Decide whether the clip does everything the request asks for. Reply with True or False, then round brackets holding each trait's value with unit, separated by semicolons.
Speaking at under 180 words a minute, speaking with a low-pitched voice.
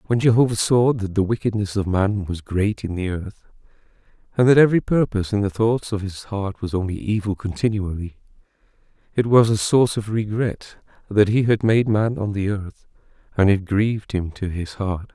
False (190 wpm; 105 Hz)